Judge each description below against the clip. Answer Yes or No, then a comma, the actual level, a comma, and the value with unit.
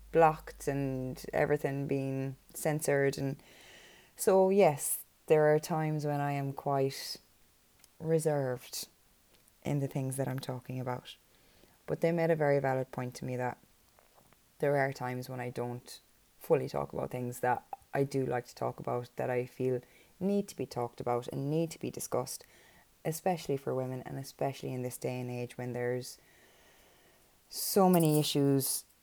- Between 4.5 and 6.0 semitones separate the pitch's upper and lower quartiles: No, average, 3.3 semitones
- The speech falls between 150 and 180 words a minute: Yes, average, 160 wpm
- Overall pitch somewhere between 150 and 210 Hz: No, low, 135 Hz